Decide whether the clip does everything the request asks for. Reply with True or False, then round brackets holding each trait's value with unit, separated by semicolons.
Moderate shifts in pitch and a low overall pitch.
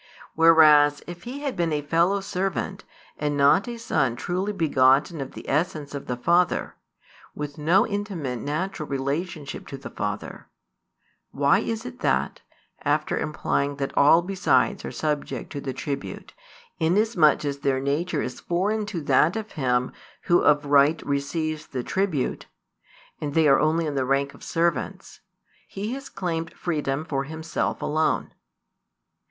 False (4.0 semitones; 155 Hz)